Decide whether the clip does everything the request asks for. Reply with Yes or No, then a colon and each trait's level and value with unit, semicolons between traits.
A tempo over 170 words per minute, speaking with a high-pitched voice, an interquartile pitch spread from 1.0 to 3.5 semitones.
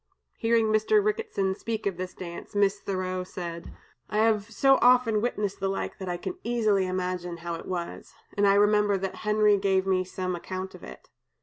Yes: average, 190 wpm; high, 200 Hz; average, 2.8 semitones